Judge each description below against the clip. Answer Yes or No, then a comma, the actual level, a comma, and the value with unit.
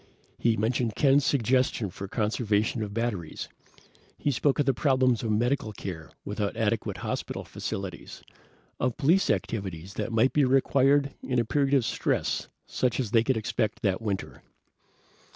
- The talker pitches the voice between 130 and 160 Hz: No, low, 115 Hz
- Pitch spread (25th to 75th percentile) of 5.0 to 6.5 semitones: No, average, 4.1 semitones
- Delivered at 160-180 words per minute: No, average, 150 wpm